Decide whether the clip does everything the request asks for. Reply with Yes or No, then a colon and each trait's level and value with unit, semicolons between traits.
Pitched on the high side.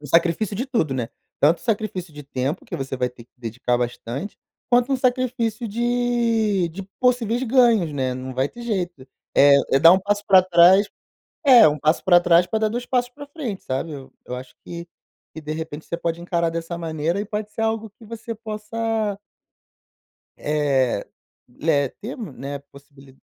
No: medium, 175 Hz